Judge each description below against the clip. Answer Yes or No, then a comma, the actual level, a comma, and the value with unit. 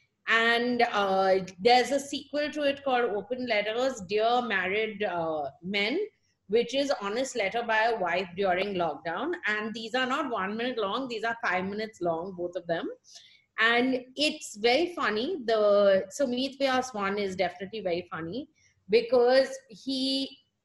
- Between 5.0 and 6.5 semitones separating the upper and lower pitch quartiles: Yes, average, 5.3 semitones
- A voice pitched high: Yes, high, 225 Hz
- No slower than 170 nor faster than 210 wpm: No, average, 155 wpm